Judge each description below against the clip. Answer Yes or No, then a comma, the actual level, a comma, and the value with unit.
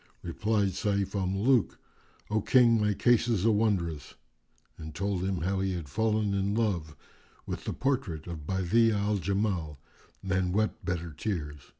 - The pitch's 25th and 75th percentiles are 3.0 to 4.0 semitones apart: Yes, average, 3.7 semitones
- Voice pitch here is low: Yes, very low, 95 Hz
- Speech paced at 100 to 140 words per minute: No, average, 160 wpm